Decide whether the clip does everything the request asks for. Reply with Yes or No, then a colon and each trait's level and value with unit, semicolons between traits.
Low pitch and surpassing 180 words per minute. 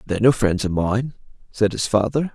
Yes: low, 110 Hz; fast, 205 wpm